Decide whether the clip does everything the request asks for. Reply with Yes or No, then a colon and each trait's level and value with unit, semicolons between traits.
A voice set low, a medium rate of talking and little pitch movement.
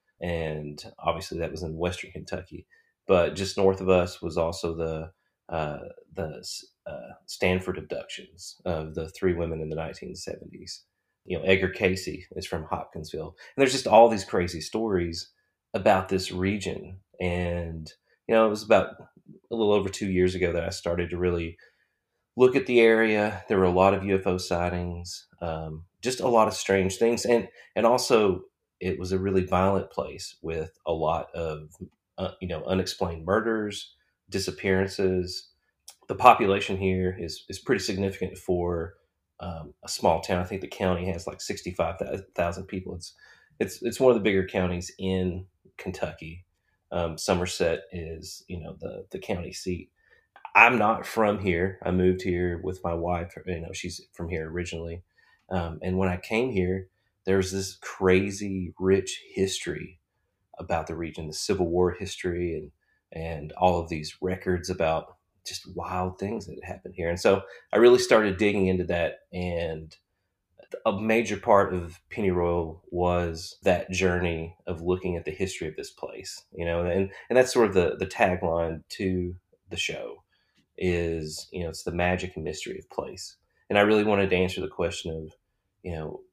Yes: very low, 90 Hz; average, 170 wpm; narrow, 2.0 semitones